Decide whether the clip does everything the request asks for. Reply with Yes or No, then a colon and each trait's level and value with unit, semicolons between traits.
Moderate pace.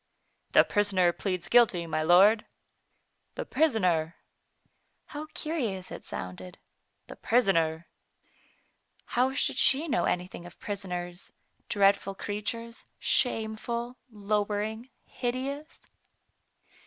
No: slow, 95 wpm